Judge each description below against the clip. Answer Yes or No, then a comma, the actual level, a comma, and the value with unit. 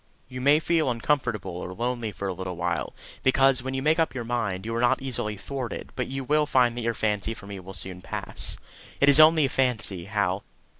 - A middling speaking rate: No, fast, 220 wpm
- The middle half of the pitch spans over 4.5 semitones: Yes, average, 5.1 semitones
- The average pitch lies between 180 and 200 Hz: No, low, 120 Hz